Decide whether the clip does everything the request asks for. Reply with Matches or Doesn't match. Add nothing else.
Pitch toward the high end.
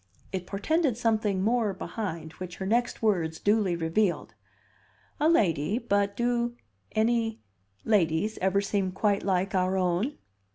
Matches